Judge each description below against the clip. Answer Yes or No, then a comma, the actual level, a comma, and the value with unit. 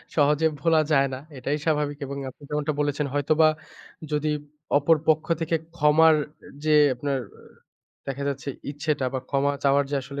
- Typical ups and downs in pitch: No, narrow, 1.7 semitones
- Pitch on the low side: No, medium, 145 Hz